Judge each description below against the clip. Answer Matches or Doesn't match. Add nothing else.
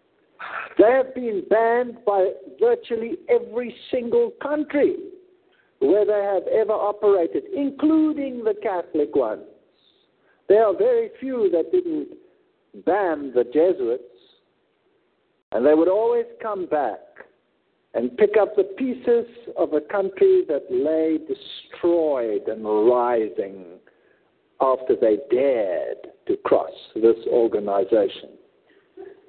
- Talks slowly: Matches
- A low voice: Doesn't match